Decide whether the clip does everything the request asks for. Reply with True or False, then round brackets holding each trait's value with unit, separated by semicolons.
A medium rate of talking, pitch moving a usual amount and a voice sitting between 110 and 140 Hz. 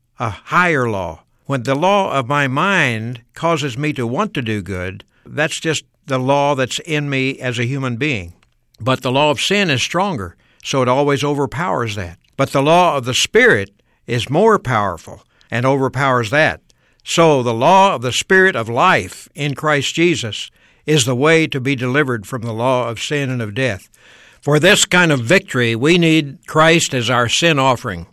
True (190 wpm; 4.1 semitones; 135 Hz)